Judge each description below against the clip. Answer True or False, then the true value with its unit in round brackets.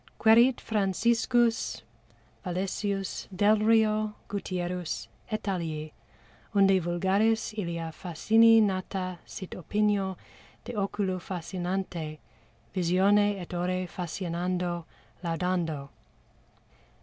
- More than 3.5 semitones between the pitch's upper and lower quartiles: False (3.0 semitones)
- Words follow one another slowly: True (80 wpm)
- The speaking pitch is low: False (190 Hz)